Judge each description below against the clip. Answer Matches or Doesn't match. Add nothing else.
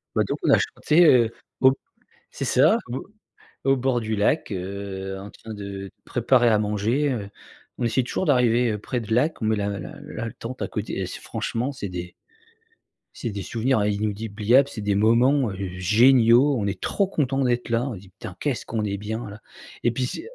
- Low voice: Matches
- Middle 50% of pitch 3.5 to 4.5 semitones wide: Matches